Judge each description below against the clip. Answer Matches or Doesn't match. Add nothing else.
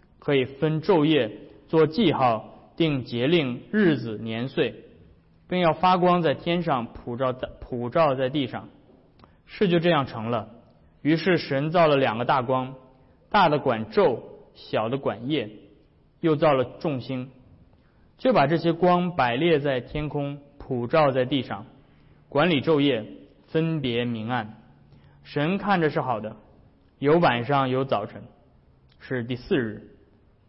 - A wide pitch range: Doesn't match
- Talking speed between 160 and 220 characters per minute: Matches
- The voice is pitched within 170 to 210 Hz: Doesn't match